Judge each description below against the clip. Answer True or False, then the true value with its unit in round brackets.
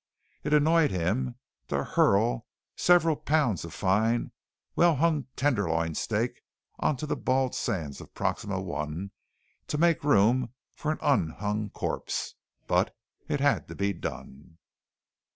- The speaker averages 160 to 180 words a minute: False (135 wpm)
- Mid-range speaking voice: False (125 Hz)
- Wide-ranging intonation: True (8.0 semitones)